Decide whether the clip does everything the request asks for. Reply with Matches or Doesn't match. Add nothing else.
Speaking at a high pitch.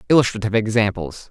Doesn't match